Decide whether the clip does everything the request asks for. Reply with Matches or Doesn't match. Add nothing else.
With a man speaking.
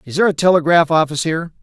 Matches